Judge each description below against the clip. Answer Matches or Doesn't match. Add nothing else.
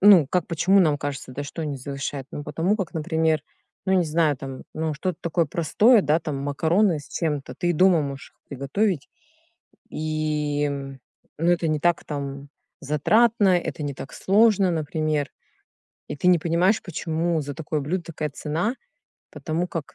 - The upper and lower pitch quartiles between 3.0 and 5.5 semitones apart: Matches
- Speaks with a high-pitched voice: Doesn't match